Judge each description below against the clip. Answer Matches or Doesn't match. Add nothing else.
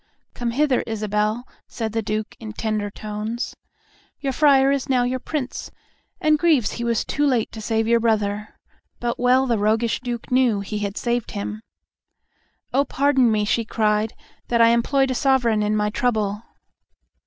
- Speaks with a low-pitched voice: Doesn't match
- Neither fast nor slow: Matches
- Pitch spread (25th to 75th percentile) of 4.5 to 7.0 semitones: Doesn't match